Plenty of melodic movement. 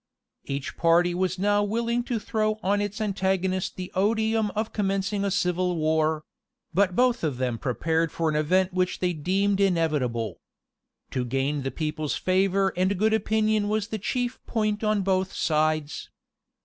No: average, 4.6 semitones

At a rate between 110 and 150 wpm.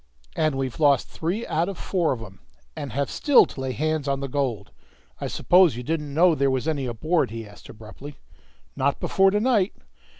No: average, 200 wpm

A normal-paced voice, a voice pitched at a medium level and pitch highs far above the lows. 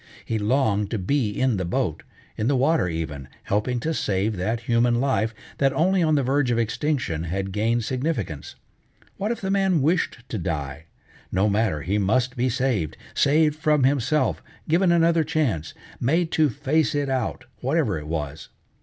No: average, 170 wpm; low, 125 Hz; wide, 6.9 semitones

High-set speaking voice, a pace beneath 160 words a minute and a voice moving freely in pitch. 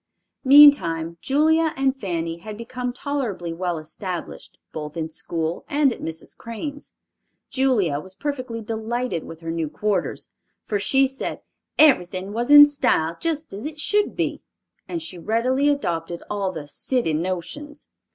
Yes: high, 220 Hz; average, 145 wpm; wide, 8.7 semitones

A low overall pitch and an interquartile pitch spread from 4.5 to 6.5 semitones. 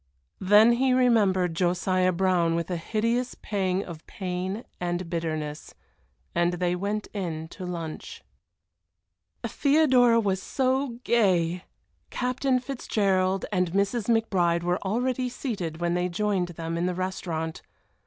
No: medium, 185 Hz; average, 4.8 semitones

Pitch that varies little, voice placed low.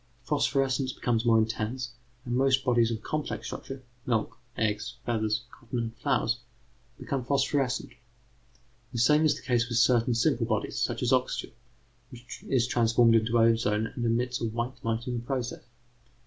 Yes: narrow, 2.1 semitones; low, 120 Hz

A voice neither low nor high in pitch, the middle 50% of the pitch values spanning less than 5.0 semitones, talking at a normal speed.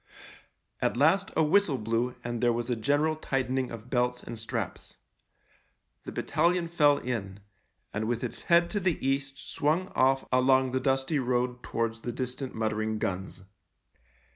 No: low, 130 Hz; average, 3.7 semitones; average, 155 wpm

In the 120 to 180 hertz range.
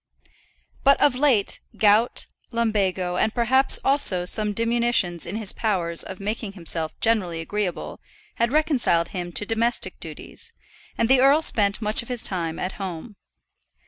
No: high, 215 Hz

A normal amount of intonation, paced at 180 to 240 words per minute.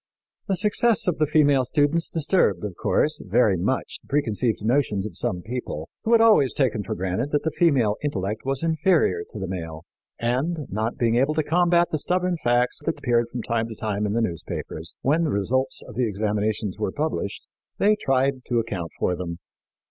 No: wide, 6.7 semitones; average, 195 wpm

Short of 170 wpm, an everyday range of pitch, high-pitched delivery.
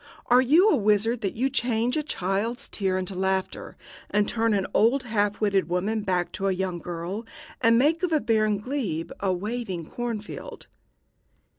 No: average, 175 wpm; average, 4.1 semitones; high, 210 Hz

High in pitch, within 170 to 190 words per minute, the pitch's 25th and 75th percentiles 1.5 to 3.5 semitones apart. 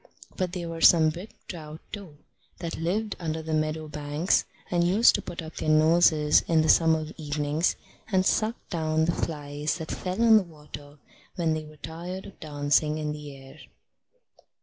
No: medium, 160 Hz; average, 175 wpm; narrow, 2.4 semitones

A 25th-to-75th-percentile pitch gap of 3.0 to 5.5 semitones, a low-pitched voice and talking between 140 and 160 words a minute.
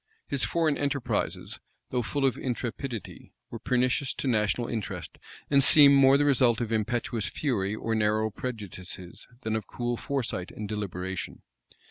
Yes: average, 4.2 semitones; low, 120 Hz; average, 145 wpm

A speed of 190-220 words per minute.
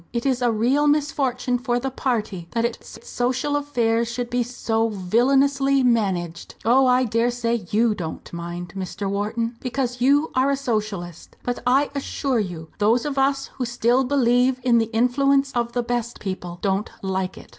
No: average, 175 wpm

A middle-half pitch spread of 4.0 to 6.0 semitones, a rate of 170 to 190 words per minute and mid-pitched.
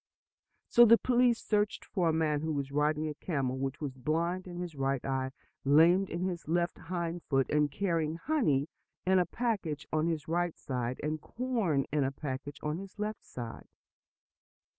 Yes: average, 4.5 semitones; average, 180 wpm; medium, 160 Hz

